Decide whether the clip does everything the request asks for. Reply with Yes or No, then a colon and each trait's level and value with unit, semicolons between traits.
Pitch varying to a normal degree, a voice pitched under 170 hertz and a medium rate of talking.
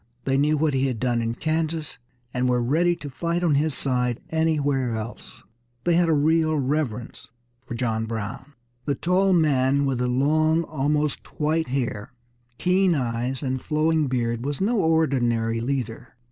Yes: average, 4.2 semitones; medium, 140 Hz; average, 160 wpm